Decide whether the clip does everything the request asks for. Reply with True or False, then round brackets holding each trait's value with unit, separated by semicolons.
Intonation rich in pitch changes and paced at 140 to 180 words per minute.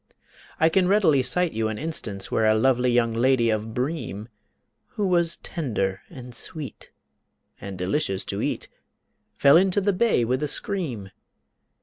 True (7.2 semitones; 150 wpm)